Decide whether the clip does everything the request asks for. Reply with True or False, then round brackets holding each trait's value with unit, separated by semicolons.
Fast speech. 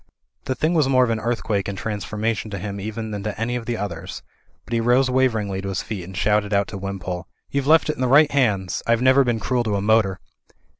True (250 wpm)